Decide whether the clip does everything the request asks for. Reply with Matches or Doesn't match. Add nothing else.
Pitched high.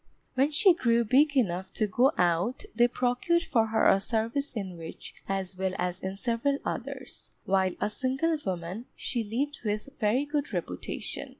Matches